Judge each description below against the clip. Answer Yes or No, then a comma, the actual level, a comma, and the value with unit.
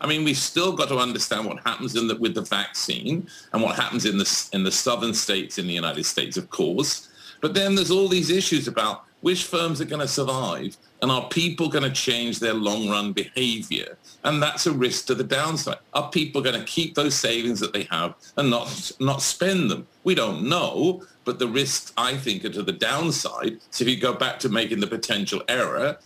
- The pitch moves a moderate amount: No, wide, 6.0 semitones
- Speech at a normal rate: No, fast, 220 wpm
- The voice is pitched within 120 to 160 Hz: Yes, medium, 140 Hz